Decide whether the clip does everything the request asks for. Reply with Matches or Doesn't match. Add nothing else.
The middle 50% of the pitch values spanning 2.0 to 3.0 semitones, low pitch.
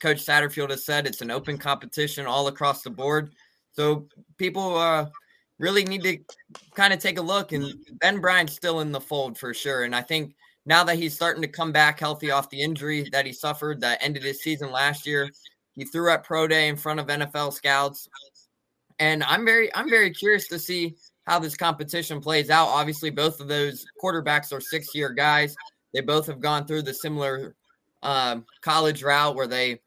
Doesn't match